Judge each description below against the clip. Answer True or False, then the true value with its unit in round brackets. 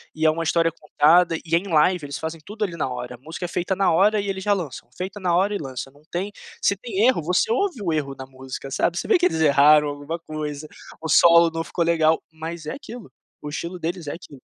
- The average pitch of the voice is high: False (165 Hz)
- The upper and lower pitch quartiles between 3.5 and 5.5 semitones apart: True (3.8 semitones)